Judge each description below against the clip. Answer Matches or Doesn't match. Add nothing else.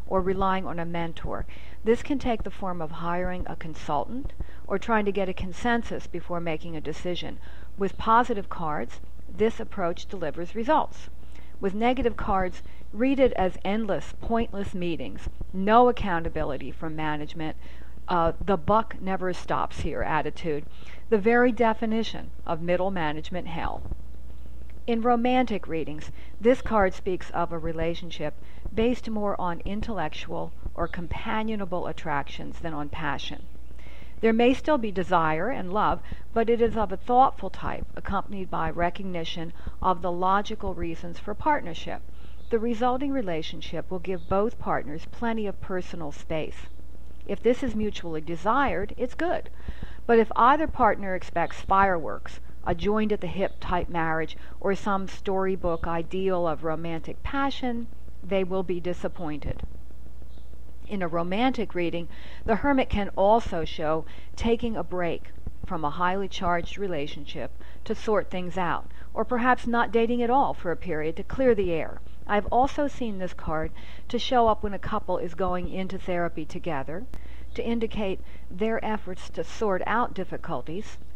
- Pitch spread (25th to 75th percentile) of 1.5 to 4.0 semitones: Doesn't match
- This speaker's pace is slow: Doesn't match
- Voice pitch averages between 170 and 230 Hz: Matches